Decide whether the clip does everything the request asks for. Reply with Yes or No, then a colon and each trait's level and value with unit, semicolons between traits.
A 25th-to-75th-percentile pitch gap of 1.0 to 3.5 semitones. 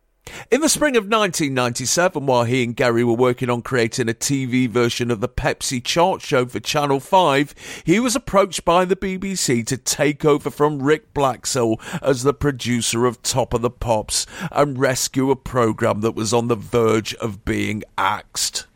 No: average, 4.1 semitones